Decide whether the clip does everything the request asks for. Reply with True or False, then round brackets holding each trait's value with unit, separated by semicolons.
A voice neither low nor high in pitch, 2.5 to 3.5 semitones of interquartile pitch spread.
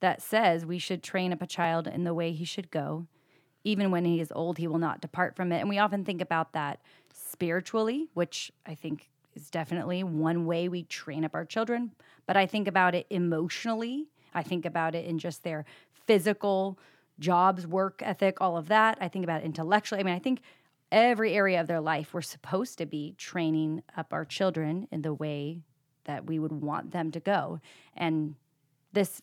True (170 Hz; 3.2 semitones)